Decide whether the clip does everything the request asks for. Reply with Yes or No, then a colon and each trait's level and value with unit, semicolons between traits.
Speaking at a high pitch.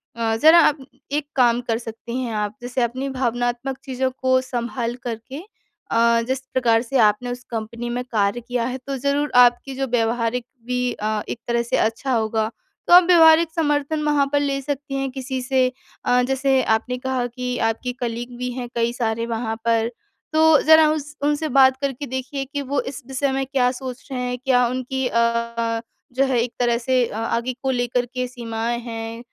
Yes: very high, 250 Hz